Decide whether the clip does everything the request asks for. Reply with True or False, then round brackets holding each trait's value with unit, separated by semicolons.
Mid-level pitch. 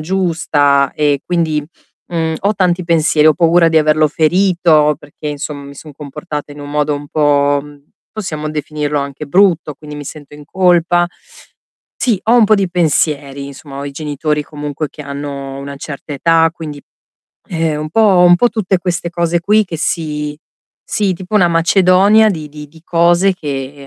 True (155 Hz)